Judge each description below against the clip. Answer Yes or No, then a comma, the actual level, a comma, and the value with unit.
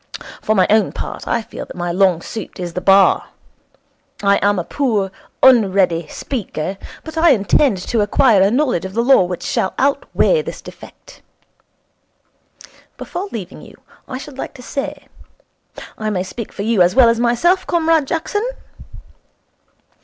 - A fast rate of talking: No, average, 160 wpm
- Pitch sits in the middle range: No, high, 220 Hz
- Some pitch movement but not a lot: No, wide, 6.2 semitones